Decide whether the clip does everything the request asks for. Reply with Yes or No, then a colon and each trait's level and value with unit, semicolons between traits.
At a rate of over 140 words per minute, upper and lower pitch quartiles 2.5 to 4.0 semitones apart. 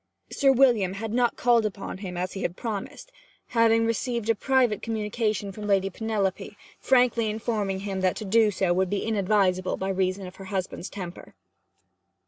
Yes: average, 170 wpm; average, 3.2 semitones